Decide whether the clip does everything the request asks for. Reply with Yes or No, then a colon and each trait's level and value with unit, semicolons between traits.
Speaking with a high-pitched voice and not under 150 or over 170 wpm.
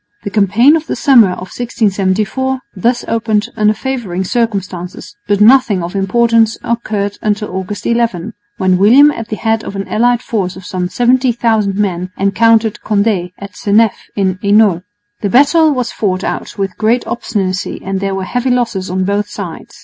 Yes: high, 210 Hz; average, 165 wpm